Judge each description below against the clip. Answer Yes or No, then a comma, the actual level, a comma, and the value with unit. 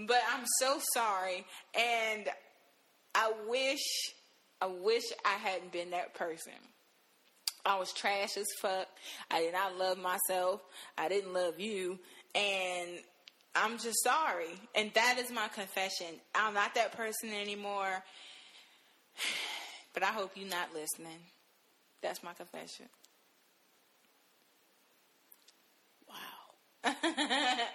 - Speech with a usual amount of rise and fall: Yes, average, 3.8 semitones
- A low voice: No, high, 200 Hz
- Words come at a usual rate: No, slow, 110 wpm